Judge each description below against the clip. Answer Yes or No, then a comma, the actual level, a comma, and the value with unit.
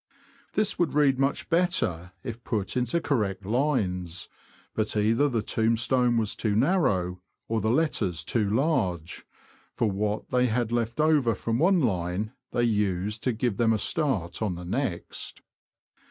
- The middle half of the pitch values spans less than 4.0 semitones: No, average, 4.8 semitones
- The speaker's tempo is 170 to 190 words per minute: No, average, 155 wpm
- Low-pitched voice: Yes, low, 115 Hz